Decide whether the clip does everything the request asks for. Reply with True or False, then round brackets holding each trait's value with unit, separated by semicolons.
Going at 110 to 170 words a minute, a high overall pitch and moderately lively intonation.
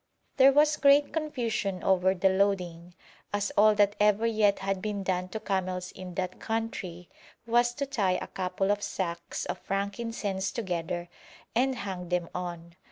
True (160 wpm; 195 Hz; 3.6 semitones)